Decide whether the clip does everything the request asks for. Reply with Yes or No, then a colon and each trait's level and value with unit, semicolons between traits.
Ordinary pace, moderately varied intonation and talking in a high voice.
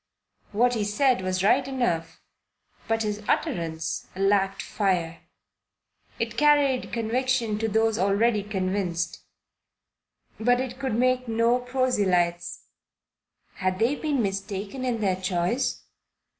No: slow, 115 wpm; average, 4.8 semitones; high, 215 Hz